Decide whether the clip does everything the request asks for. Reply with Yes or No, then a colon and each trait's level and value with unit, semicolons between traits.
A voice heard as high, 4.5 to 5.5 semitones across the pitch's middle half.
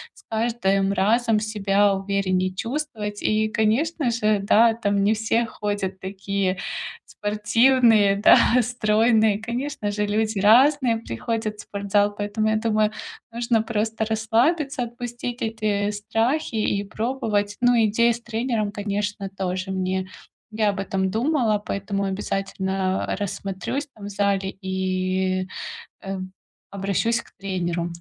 No: high, 210 Hz; narrow, 2.5 semitones